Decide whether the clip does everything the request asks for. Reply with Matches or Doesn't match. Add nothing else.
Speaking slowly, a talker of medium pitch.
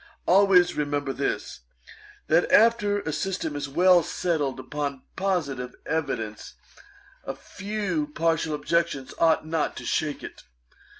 Matches